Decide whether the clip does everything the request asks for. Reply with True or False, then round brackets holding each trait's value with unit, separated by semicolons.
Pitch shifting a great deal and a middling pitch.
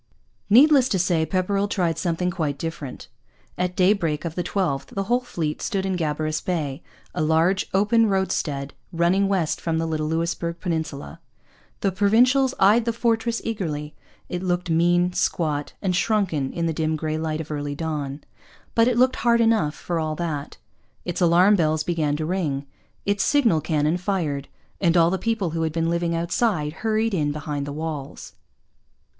False (4.1 semitones; 170 Hz)